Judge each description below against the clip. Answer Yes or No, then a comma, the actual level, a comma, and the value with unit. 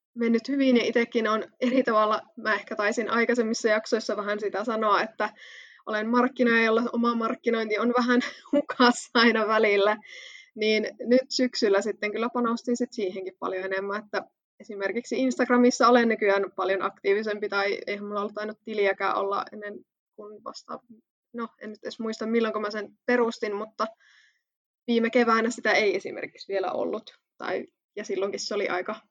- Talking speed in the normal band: No, fast, 160 wpm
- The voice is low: No, high, 225 Hz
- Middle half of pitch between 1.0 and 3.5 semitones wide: Yes, narrow, 2.5 semitones